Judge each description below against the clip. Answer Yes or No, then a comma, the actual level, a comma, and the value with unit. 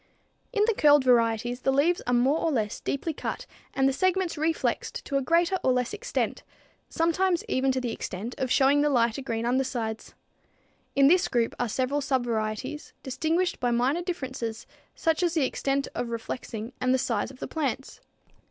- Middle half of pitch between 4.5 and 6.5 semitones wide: Yes, average, 4.8 semitones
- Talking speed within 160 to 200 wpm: Yes, average, 170 wpm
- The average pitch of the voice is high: Yes, very high, 265 Hz